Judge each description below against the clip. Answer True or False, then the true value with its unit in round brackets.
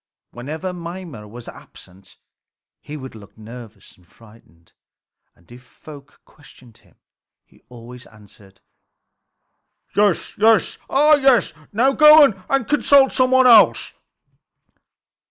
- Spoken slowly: True (110 wpm)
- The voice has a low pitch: False (150 Hz)